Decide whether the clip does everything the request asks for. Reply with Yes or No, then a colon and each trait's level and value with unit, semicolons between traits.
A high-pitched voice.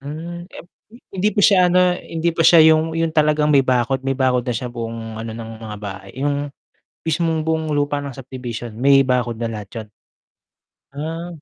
No: medium, 140 Hz